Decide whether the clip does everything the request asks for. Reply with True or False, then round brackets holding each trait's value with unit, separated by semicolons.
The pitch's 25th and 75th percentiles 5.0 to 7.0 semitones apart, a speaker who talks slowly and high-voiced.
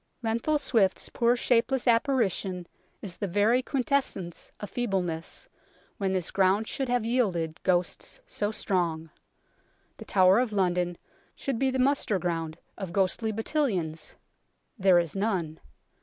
True (5.3 semitones; 130 wpm; 200 Hz)